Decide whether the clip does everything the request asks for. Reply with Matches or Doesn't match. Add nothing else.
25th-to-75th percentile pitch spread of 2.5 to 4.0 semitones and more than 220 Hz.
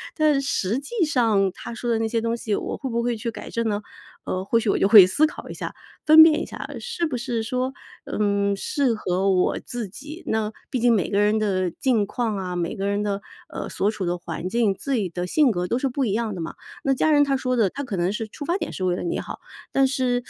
Doesn't match